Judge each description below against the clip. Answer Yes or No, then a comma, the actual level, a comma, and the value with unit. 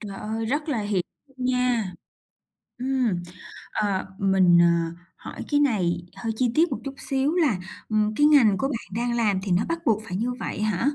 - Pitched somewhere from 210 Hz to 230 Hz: Yes, high, 225 Hz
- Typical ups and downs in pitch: Yes, average, 5.0 semitones